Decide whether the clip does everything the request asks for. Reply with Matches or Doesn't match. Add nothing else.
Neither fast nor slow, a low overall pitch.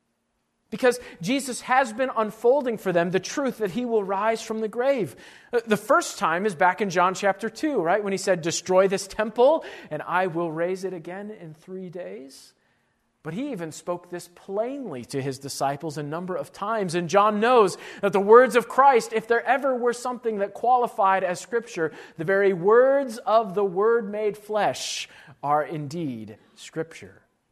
Doesn't match